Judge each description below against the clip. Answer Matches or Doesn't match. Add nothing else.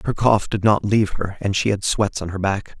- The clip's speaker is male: Matches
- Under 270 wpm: Doesn't match